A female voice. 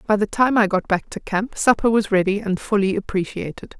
Yes: female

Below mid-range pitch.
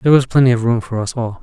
Yes: low, 120 Hz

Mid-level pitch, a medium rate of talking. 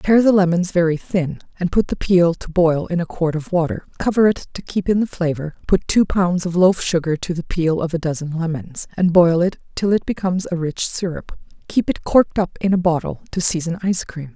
No: medium, 175 Hz; fast, 235 wpm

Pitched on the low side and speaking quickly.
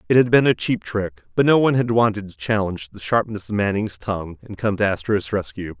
Yes: low, 105 Hz; fast, 240 wpm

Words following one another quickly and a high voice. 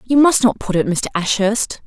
Yes: fast, 225 wpm; high, 220 Hz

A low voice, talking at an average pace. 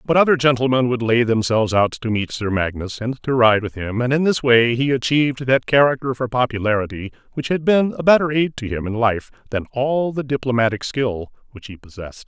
No: low, 125 Hz; fast, 215 wpm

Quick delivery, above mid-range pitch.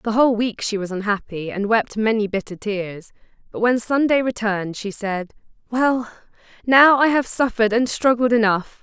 No: average, 170 wpm; high, 220 Hz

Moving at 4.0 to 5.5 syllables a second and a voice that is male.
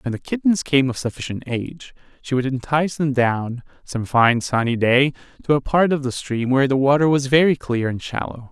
Yes: 5.4 syllables/s; male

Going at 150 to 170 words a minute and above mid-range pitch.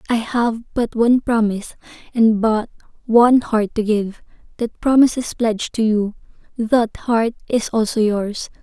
Yes: average, 155 wpm; high, 225 Hz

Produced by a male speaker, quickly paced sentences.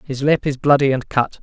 Yes: male; fast, 250 wpm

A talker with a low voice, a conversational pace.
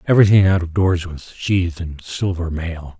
Yes: very low, 85 Hz; average, 180 wpm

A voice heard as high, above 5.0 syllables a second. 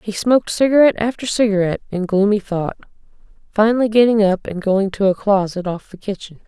Yes: high, 205 Hz; 6.0 syllables/s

